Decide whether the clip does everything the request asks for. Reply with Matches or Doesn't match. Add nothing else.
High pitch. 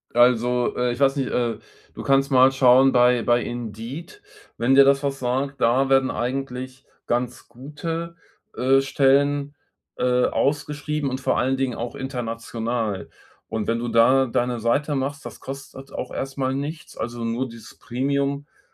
Doesn't match